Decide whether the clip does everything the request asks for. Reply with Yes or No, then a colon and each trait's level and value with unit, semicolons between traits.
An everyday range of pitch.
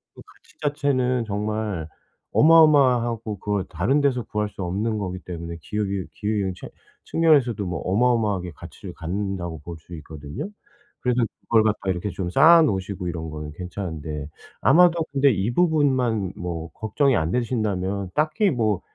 No: wide, 6.0 semitones